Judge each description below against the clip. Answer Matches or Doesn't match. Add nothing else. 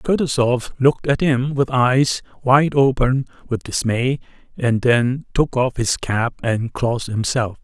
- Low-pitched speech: Matches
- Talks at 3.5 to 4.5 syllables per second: Matches